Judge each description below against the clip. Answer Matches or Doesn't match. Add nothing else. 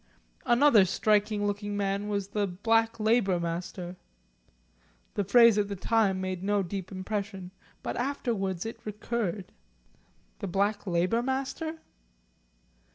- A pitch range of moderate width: Matches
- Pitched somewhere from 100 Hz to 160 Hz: Doesn't match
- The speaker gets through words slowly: Matches